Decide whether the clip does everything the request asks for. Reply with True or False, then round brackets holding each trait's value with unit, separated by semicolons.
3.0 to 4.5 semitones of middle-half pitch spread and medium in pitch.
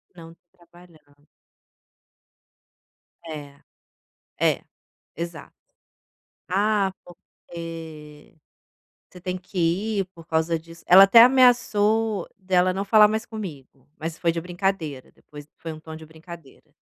True (3.5 semitones; 170 Hz)